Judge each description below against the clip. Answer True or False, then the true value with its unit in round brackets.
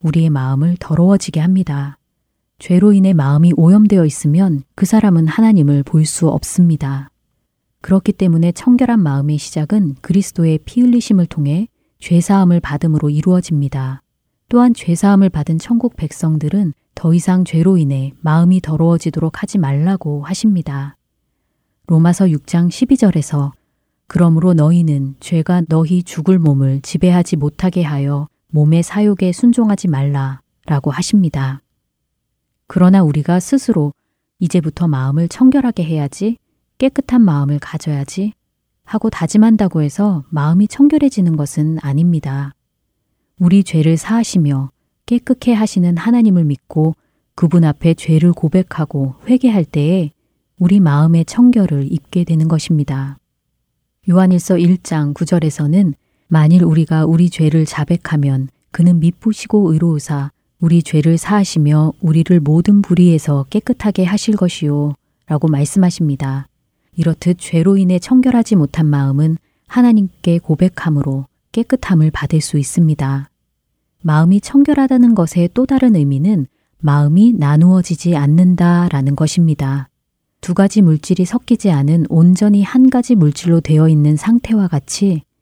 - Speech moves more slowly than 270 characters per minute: False (310 characters per minute)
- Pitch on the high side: False (170 Hz)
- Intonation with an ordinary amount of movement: True (4.1 semitones)